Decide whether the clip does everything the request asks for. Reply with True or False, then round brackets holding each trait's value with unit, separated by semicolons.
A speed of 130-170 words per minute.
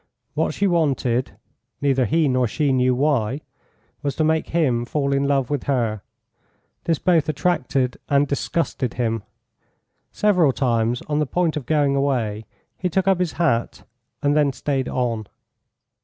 True (155 wpm)